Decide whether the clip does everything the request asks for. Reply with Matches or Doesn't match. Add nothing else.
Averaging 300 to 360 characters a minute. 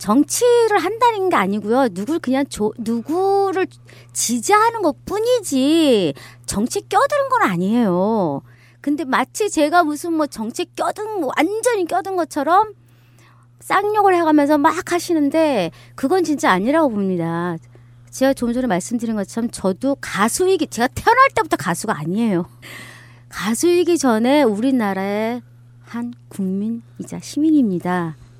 Doesn't match